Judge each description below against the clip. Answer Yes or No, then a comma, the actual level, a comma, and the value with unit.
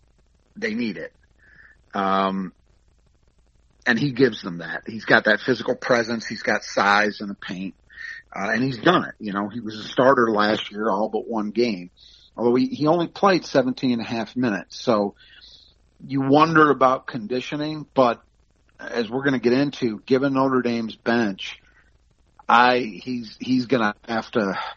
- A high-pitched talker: No, low, 120 Hz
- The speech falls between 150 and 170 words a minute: Yes, average, 165 wpm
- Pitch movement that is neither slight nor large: Yes, average, 4.1 semitones